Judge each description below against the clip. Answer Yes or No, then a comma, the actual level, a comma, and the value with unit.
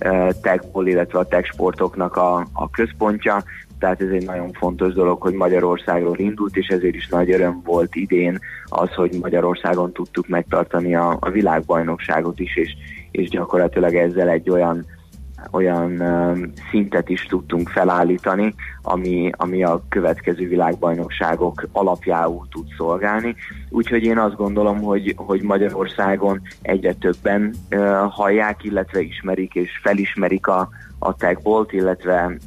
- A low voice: Yes, very low, 90 Hz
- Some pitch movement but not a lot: No, narrow, 2.0 semitones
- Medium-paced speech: Yes, average, 130 wpm